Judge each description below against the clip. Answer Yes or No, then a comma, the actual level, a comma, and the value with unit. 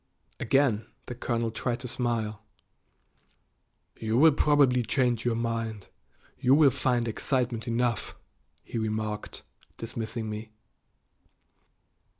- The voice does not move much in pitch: Yes, narrow, 2.2 semitones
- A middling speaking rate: No, slow, 105 wpm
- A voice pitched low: Yes, low, 115 Hz